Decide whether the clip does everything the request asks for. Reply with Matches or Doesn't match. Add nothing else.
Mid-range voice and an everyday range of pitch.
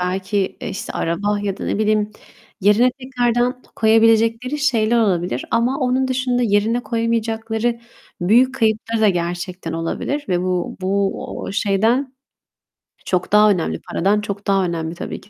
Doesn't match